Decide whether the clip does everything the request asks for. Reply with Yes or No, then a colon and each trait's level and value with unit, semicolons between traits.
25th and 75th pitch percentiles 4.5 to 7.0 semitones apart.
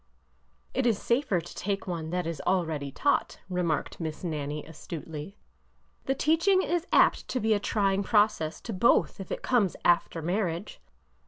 Yes: average, 5.2 semitones